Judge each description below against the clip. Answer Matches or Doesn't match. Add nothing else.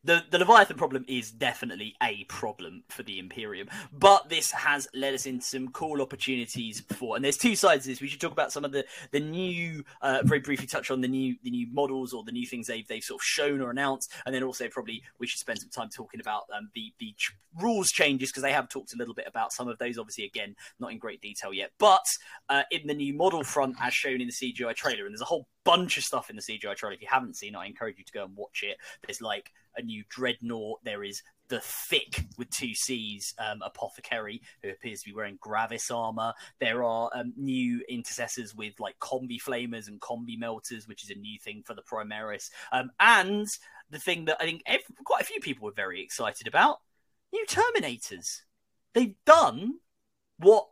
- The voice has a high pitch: Doesn't match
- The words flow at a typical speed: Doesn't match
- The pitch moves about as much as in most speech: Doesn't match